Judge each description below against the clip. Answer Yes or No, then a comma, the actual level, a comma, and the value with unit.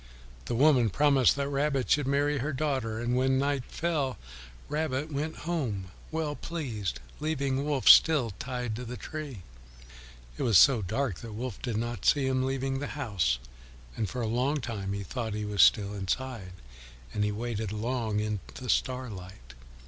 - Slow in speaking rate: No, average, 170 wpm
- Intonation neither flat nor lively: Yes, average, 4.6 semitones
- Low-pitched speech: Yes, low, 125 Hz